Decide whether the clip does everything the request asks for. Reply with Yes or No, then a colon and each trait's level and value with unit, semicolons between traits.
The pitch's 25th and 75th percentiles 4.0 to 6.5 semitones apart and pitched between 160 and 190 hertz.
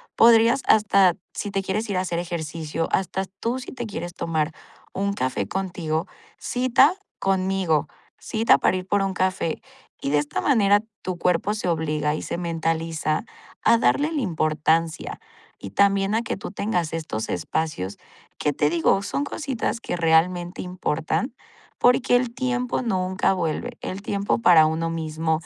Yes: average, 4.6 semitones; medium, 185 Hz